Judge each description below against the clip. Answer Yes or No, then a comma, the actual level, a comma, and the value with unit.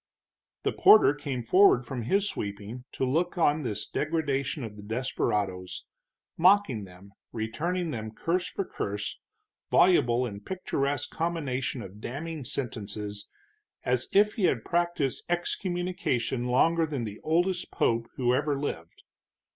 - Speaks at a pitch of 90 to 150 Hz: Yes, low, 135 Hz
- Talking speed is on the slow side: Yes, slow, 130 wpm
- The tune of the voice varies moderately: No, wide, 7.2 semitones